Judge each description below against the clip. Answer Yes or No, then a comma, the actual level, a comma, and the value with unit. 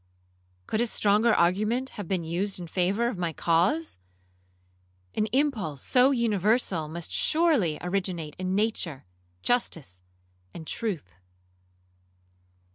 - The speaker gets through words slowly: Yes, slow, 115 wpm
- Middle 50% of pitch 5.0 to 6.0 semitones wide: Yes, wide, 5.4 semitones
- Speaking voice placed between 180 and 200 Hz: Yes, high, 190 Hz